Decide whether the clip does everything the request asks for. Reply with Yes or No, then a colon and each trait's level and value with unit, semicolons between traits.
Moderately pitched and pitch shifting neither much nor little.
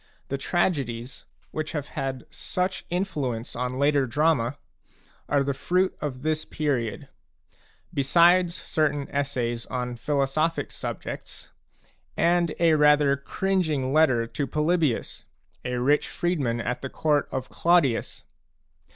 Yes: medium, 145 Hz; average, 3.9 semitones